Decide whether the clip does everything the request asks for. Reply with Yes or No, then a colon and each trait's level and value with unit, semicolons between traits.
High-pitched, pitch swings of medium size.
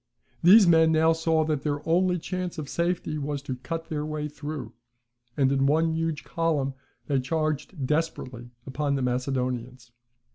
No: medium, 150 Hz; average, 3.2 semitones